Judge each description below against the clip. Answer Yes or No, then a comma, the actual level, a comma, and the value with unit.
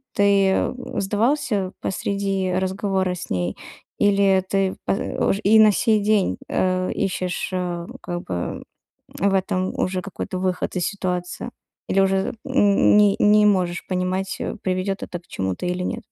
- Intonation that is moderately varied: No, narrow, 1.7 semitones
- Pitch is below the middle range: No, high, 190 Hz